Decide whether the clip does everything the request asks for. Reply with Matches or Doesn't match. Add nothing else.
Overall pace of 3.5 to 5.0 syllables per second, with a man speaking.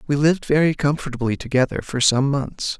Doesn't match